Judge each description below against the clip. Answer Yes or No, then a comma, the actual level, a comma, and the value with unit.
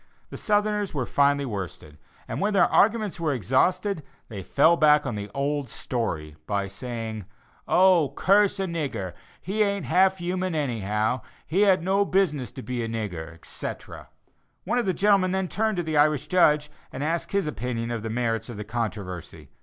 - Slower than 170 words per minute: No, average, 175 wpm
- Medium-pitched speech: Yes, medium, 145 Hz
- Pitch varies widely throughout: Yes, wide, 8.6 semitones